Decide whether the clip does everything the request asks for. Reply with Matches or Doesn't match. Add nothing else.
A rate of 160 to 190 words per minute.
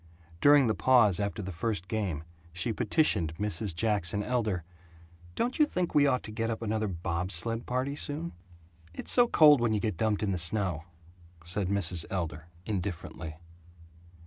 Matches